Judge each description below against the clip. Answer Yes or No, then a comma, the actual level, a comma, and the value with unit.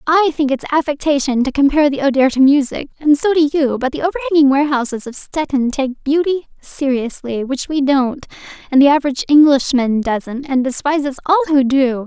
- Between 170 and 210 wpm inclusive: Yes, average, 180 wpm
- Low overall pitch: No, very high, 280 Hz